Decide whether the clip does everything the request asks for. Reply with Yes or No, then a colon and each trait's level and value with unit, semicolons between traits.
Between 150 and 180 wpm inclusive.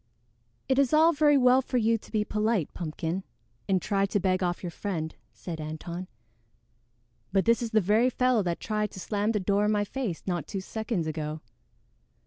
No: average, 190 wpm